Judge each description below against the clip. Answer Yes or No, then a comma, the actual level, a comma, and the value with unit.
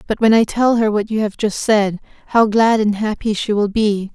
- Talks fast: Yes, fast, 245 wpm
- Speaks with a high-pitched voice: Yes, high, 215 Hz